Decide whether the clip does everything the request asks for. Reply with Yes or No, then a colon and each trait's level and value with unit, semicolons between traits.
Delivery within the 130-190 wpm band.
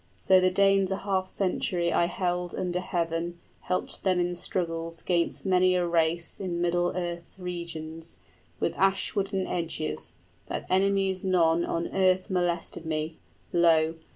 Yes: average, 150 wpm